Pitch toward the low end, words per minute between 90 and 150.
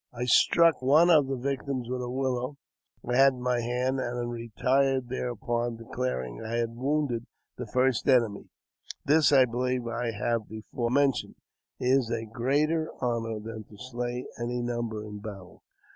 No: low, 125 Hz; average, 160 wpm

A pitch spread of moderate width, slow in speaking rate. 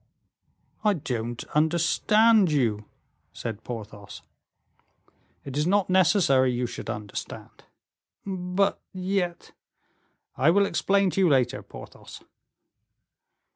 No: wide, 7.9 semitones; slow, 100 wpm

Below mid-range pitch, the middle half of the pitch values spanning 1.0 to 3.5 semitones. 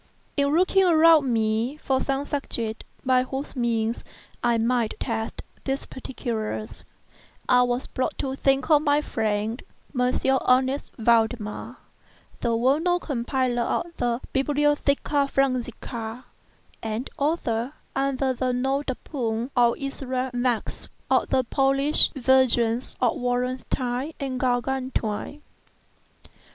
No: very high, 255 Hz; narrow, 2.6 semitones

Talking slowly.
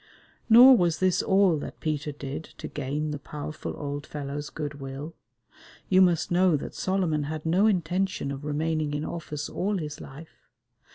No: average, 165 wpm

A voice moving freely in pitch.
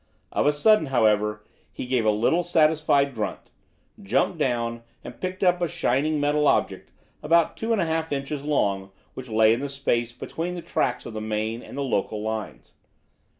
Yes: wide, 6.4 semitones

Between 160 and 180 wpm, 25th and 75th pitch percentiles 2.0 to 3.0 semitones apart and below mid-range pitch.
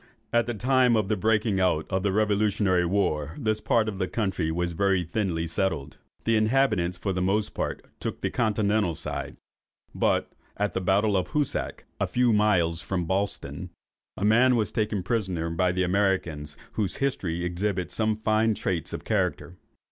No: average, 170 wpm; average, 3.5 semitones; low, 100 Hz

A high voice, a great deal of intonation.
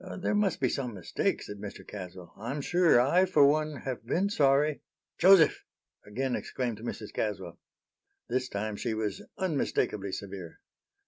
No: low, 125 Hz; wide, 6.7 semitones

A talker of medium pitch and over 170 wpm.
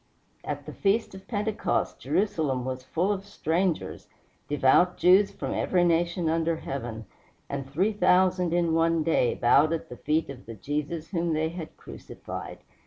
No: medium, 165 Hz; average, 160 wpm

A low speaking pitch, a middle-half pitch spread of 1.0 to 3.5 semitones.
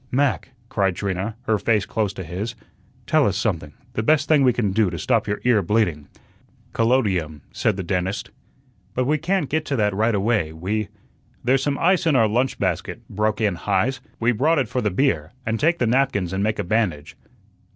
No: low, 110 Hz; average, 5.2 semitones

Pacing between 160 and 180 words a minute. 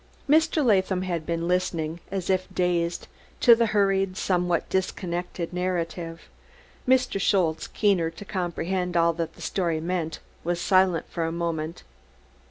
No: average, 140 wpm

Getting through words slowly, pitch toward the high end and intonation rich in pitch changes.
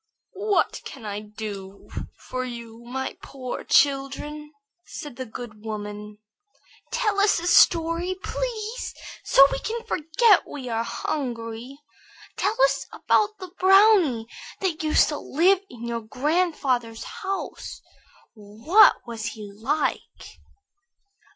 Yes: slow, 120 wpm; very high, 275 Hz; wide, 8.4 semitones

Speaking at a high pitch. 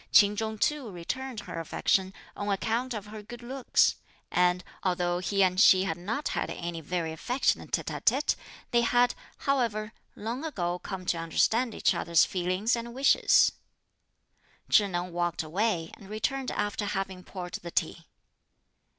Yes: high, 200 Hz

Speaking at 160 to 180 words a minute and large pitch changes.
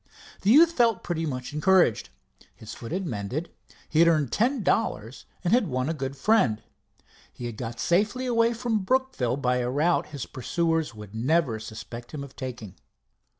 Yes: average, 175 wpm; wide, 8.2 semitones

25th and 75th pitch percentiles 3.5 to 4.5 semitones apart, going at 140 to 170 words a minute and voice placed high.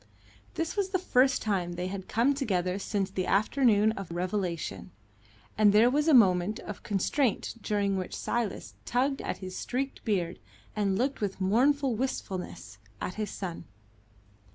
No: wide, 5.4 semitones; average, 155 wpm; high, 205 Hz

